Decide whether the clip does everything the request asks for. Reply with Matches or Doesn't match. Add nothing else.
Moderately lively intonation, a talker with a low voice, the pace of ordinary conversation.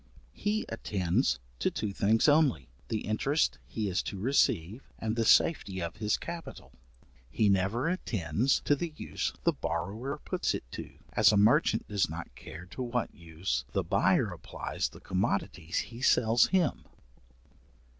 Doesn't match